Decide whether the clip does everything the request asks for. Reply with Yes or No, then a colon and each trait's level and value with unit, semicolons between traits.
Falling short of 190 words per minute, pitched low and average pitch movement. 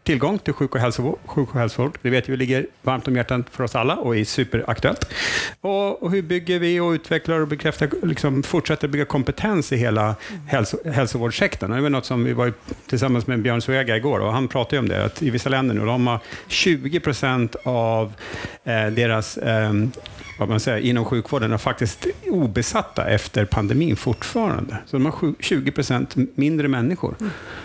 Yes: average, 180 wpm; low, 130 Hz; average, 4.0 semitones